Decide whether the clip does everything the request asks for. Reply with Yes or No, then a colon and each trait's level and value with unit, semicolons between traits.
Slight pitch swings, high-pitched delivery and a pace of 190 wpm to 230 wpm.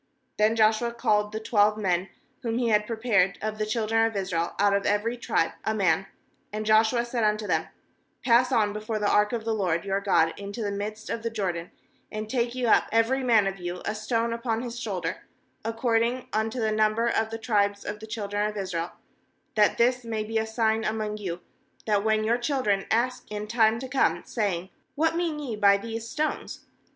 Yes: narrow, 2.1 semitones; high, 215 Hz; fast, 205 wpm